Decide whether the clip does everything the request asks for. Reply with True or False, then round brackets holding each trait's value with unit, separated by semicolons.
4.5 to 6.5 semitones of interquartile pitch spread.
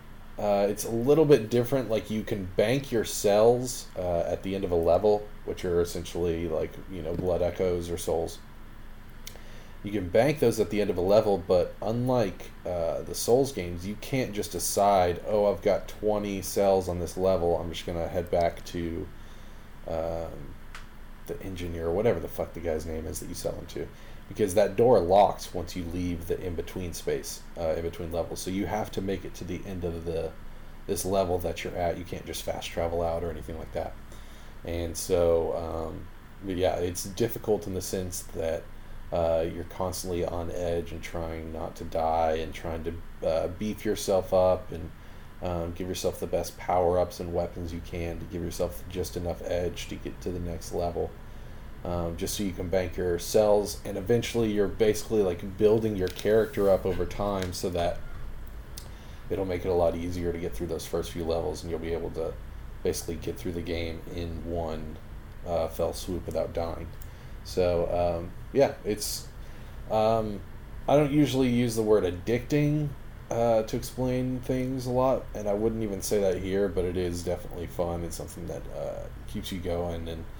False (3.8 semitones)